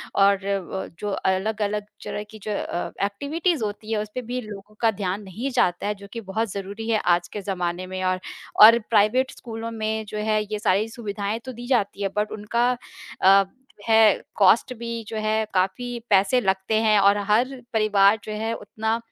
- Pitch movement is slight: Yes, narrow, 2.3 semitones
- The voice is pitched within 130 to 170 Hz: No, high, 210 Hz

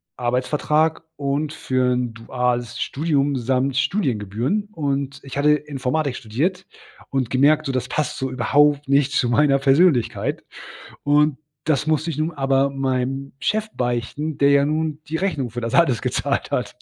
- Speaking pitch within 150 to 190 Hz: No, medium, 140 Hz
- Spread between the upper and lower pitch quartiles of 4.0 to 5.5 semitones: No, average, 3.0 semitones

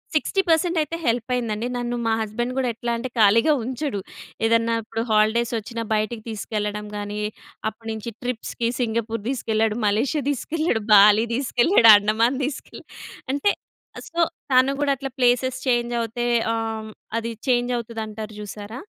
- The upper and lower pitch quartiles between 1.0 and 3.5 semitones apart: Yes, narrow, 2.5 semitones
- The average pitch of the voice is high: Yes, high, 230 Hz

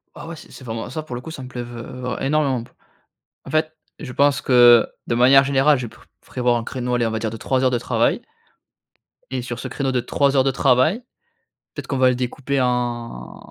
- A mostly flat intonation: Yes, narrow, 2.2 semitones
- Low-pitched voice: Yes, low, 125 Hz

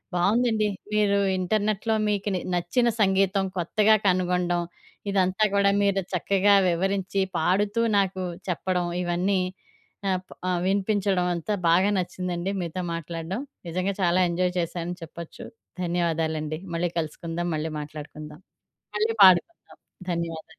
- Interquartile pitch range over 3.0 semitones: No, average, 2.7 semitones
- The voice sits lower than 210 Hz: Yes, medium, 185 Hz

